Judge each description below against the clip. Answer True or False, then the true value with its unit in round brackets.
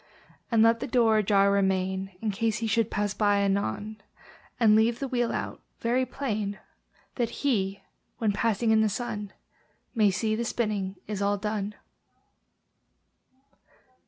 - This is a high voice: True (215 Hz)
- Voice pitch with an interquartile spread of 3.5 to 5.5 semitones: False (2.4 semitones)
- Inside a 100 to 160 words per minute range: True (145 wpm)